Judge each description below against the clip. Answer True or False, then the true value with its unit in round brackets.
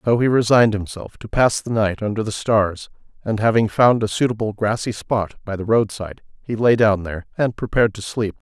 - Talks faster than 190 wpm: True (205 wpm)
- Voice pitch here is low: True (110 Hz)